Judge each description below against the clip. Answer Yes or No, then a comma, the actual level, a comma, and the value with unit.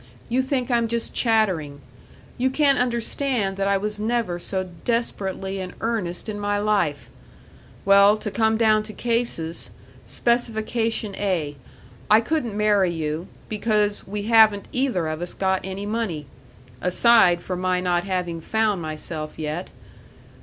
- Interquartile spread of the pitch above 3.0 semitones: Yes, average, 4.0 semitones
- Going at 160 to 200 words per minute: No, average, 140 wpm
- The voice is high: Yes, high, 205 Hz